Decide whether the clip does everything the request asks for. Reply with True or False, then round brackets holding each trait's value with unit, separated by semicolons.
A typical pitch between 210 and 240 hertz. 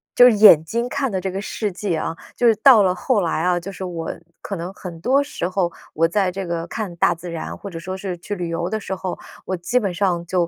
False (185 Hz)